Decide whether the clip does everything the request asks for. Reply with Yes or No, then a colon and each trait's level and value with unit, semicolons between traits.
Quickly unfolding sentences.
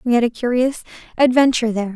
No: average, 185 wpm